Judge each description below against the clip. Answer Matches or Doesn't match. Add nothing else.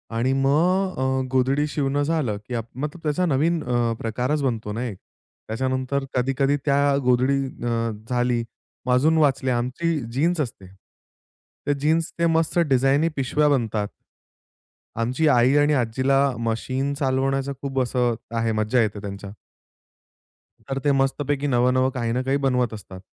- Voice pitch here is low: Matches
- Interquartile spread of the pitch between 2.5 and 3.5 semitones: Matches